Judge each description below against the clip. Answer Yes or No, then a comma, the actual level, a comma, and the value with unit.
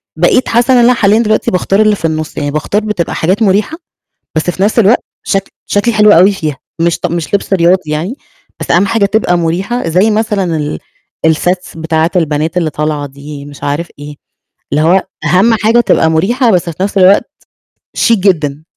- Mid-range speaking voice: Yes, medium, 180 Hz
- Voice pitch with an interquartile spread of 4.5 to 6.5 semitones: Yes, average, 4.8 semitones